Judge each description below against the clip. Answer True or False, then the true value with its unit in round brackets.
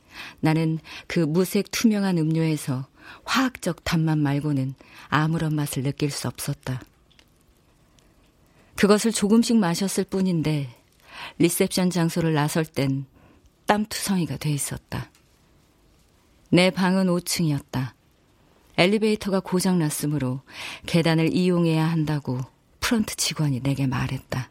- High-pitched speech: False (160 Hz)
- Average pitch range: True (4.9 semitones)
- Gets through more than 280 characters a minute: False (250 characters per minute)